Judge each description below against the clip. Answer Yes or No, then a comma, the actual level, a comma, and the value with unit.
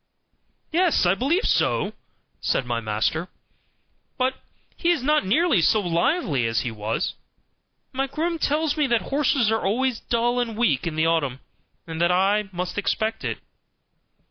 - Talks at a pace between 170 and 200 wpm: No, average, 155 wpm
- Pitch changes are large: Yes, wide, 8.7 semitones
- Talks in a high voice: Yes, high, 220 Hz